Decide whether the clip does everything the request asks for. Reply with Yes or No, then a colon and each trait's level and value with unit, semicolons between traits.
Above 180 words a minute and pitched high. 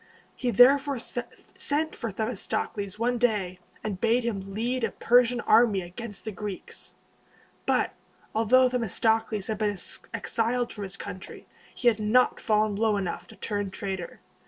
No: average, 145 wpm; high, 220 Hz